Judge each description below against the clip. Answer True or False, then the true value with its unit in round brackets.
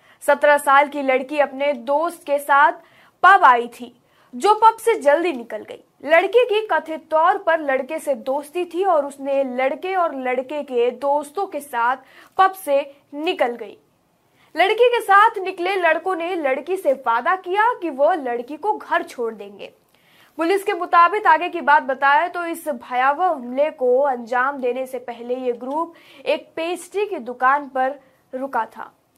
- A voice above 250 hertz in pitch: True (295 Hz)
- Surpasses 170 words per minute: False (165 wpm)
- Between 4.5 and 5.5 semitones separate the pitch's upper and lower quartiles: True (4.9 semitones)